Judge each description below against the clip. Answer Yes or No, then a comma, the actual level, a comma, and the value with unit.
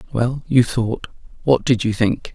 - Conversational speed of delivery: Yes, average, 155 wpm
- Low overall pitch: Yes, low, 120 Hz